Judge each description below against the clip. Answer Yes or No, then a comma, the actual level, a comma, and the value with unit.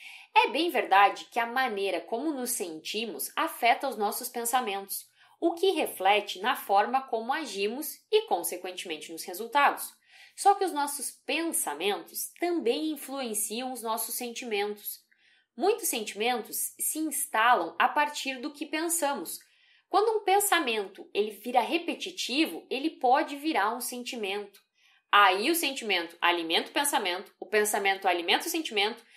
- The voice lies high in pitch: Yes, very high, 270 Hz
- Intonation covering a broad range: Yes, wide, 8.2 semitones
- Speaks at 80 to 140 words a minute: Yes, average, 135 wpm